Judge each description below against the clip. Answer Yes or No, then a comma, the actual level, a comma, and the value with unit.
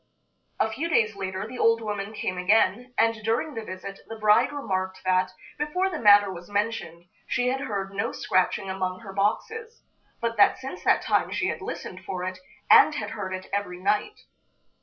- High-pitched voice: Yes, high, 205 Hz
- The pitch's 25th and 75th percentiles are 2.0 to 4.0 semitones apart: Yes, average, 3.4 semitones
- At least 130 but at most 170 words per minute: No, average, 185 wpm